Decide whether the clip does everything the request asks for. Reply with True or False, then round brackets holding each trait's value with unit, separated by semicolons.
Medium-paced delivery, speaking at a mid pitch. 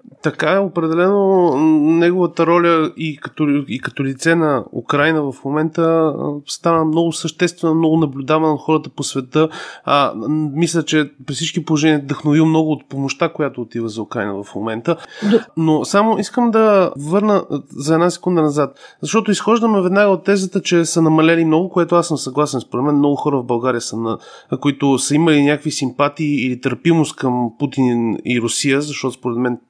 False (170 wpm; 155 Hz)